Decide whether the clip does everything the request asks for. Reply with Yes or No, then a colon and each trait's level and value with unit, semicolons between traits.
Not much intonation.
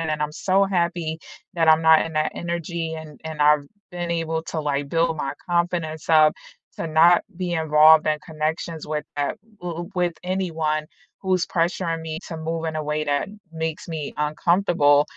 Yes: narrow, 1.8 semitones